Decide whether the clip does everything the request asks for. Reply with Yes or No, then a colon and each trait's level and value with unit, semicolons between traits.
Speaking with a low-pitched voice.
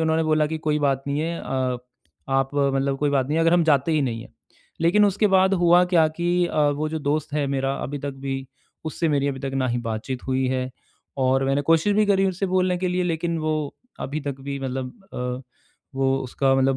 No: medium, 145 Hz